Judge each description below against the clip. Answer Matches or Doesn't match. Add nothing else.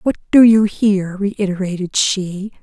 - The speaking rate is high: Doesn't match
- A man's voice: Doesn't match